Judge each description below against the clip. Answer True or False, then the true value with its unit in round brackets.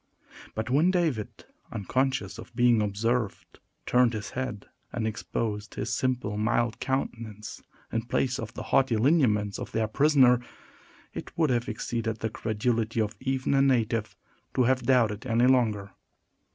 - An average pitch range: True (3.0 semitones)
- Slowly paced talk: False (145 wpm)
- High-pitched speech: False (120 Hz)